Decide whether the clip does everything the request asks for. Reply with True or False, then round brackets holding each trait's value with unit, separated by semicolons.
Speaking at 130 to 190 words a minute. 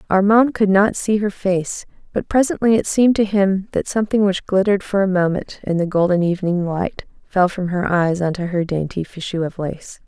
False (200 wpm)